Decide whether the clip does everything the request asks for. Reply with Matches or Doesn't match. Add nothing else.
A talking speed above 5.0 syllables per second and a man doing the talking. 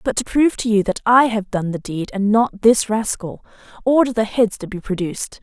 Doesn't match